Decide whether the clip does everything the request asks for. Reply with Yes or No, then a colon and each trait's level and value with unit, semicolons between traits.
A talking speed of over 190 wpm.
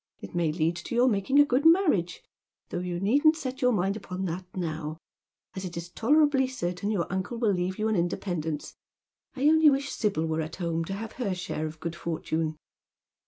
Yes: average, 200 wpm